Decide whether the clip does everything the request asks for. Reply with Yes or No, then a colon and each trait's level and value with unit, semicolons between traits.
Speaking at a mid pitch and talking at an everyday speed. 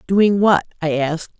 Yes: medium, 180 Hz; average, 170 wpm